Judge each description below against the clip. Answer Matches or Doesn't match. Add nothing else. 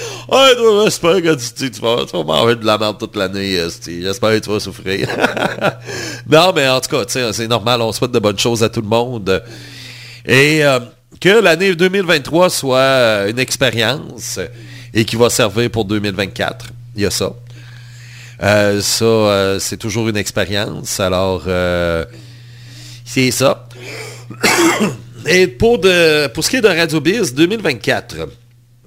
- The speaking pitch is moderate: Doesn't match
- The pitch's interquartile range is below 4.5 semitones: Matches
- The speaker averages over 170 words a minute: Doesn't match